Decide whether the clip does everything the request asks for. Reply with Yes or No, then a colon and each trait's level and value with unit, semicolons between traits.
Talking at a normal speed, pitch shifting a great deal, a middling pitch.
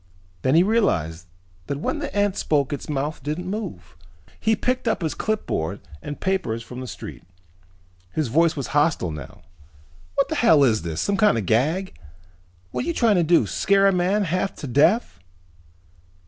Yes: average, 180 wpm; wide, 7.9 semitones; medium, 160 Hz